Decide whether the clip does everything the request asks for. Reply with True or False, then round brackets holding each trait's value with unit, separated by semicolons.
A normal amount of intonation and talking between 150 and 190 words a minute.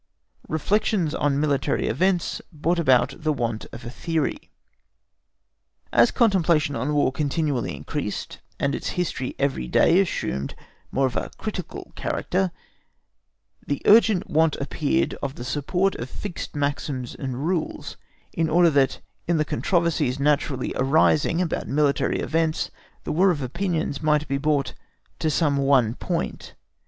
False (3.8 semitones; 140 wpm)